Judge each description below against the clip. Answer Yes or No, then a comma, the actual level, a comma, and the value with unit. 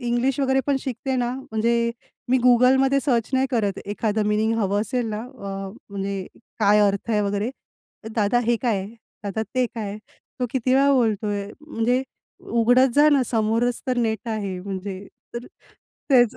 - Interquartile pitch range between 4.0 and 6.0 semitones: No, average, 3.6 semitones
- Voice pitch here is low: No, high, 230 Hz